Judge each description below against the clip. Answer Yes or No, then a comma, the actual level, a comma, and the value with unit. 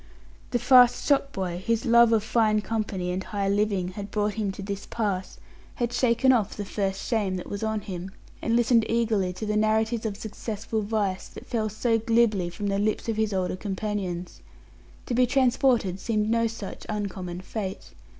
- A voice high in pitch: Yes, high, 215 Hz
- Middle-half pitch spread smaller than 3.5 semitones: Yes, average, 2.8 semitones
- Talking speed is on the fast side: No, average, 180 wpm